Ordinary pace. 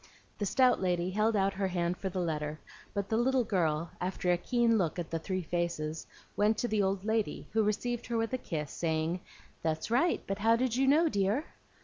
No: fast, 215 wpm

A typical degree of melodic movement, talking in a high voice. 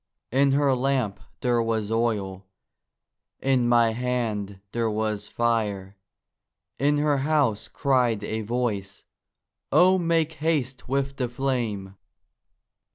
No: average, 4.2 semitones; low, 120 Hz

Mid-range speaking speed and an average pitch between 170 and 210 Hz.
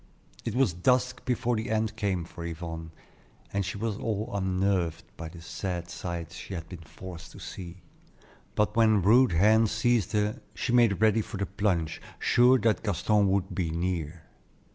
No: average, 170 wpm; low, 100 Hz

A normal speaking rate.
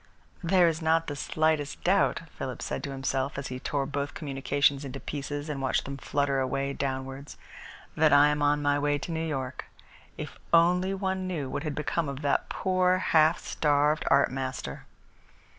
Yes: average, 175 wpm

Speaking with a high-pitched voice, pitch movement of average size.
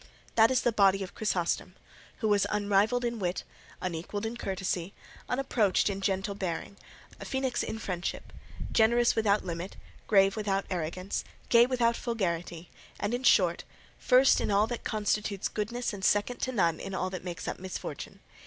Yes: high, 200 Hz; average, 3.5 semitones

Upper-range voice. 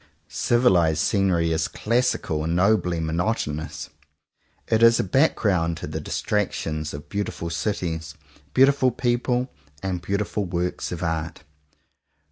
No: very low, 90 Hz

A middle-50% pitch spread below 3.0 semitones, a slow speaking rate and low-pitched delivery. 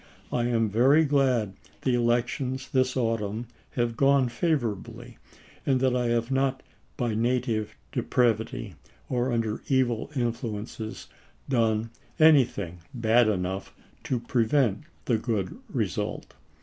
Yes: narrow, 2.6 semitones; slow, 115 wpm; low, 120 Hz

